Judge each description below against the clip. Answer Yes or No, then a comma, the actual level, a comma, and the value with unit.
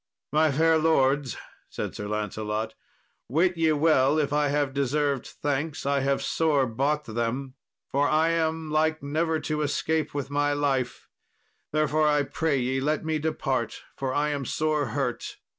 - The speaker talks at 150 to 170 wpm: Yes, average, 160 wpm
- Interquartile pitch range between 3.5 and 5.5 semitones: No, narrow, 2.5 semitones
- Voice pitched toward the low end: No, medium, 145 Hz